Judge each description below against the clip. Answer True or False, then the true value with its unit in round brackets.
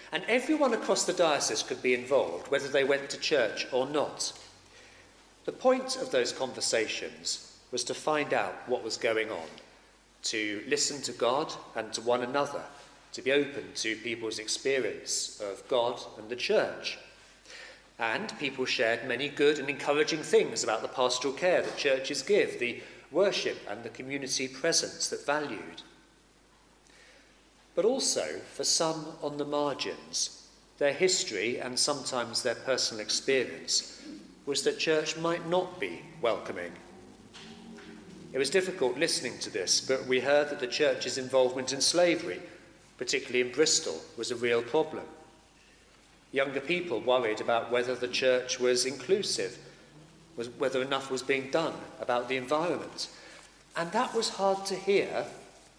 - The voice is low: False (145 Hz)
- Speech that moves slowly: False (145 wpm)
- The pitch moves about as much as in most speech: False (6.3 semitones)